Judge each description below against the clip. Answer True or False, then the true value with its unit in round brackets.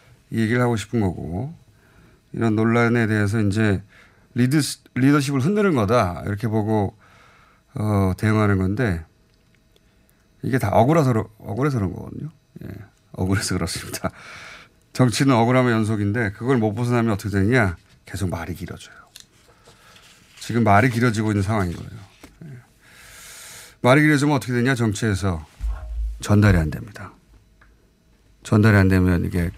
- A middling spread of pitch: True (4.1 semitones)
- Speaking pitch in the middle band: False (110 Hz)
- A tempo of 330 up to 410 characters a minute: False (295 characters per minute)